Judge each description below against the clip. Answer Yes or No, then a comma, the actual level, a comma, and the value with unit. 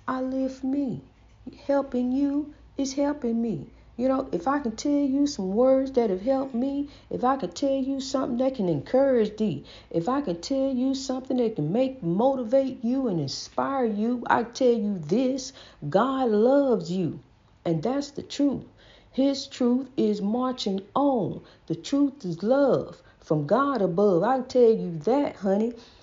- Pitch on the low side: No, very high, 255 Hz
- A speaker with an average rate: Yes, average, 170 wpm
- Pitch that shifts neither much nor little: Yes, average, 4.8 semitones